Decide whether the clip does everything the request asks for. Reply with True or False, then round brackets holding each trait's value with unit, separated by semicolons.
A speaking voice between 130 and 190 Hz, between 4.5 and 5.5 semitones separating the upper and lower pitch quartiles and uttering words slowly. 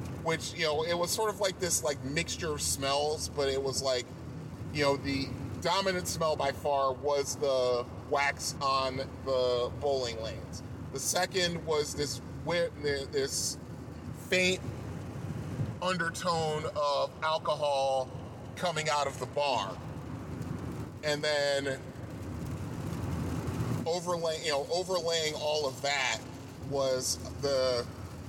False (140 Hz; 3.5 semitones; 120 wpm)